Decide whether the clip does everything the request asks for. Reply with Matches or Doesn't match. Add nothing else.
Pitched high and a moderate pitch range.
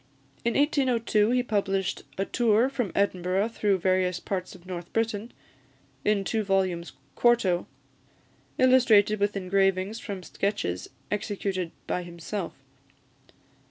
Matches